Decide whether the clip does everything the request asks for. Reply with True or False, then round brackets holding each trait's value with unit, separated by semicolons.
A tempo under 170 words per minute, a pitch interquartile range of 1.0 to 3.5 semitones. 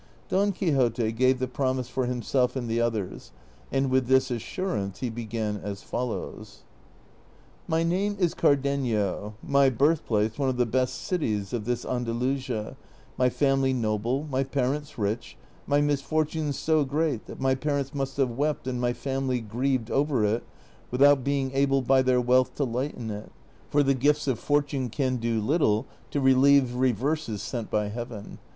True (160 wpm; 3.1 semitones)